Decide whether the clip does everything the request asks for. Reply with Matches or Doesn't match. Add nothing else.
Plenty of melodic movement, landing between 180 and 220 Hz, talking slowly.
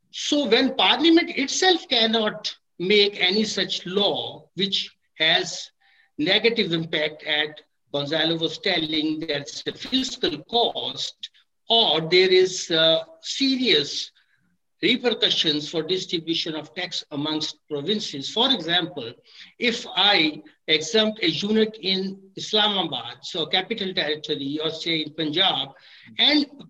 Matches